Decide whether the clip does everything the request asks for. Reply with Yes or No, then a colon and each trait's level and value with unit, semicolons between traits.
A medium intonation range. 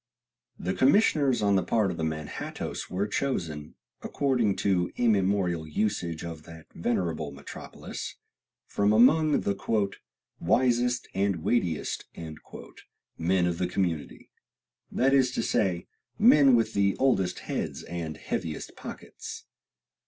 No: wide, 6.2 semitones